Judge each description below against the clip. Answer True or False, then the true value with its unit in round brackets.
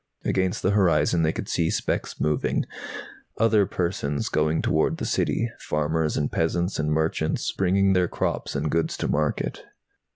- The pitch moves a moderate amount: True (3.4 semitones)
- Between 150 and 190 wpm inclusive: True (155 wpm)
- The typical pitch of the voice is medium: False (80 Hz)